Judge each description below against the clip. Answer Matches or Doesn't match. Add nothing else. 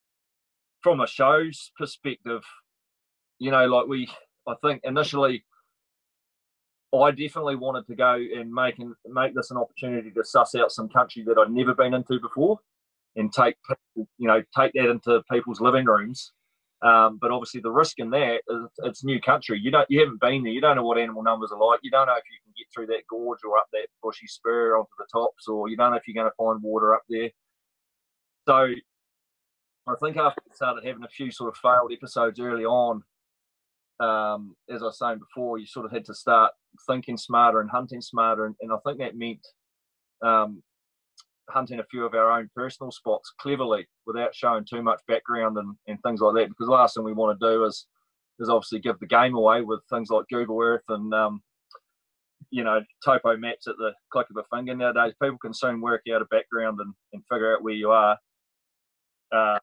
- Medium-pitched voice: Doesn't match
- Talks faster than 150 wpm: Matches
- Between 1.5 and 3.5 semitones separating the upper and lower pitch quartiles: Matches